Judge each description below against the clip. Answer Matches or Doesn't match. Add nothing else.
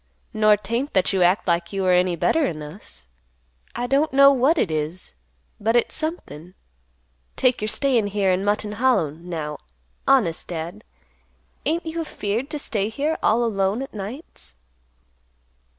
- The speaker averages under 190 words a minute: Matches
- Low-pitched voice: Doesn't match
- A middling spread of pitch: Doesn't match